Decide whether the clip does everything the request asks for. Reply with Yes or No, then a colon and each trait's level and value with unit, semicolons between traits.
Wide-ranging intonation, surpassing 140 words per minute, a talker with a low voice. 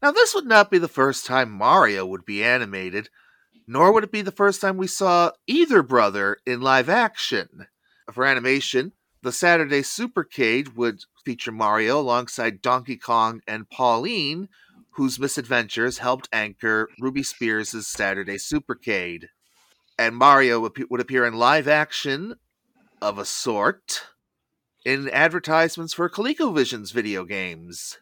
No: wide, 6.9 semitones; slow, 135 wpm; low, 130 Hz